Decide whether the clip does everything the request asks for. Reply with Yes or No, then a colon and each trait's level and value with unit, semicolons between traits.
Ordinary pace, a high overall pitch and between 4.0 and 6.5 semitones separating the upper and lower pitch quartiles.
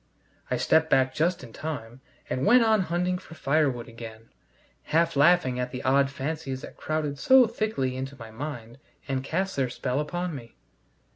No: average, 170 wpm; medium, 140 Hz; average, 4.6 semitones